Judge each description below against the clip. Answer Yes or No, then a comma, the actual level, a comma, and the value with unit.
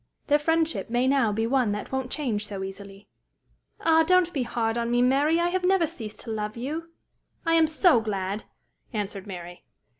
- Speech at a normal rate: Yes, average, 185 wpm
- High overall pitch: Yes, high, 245 Hz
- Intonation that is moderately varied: No, wide, 7.2 semitones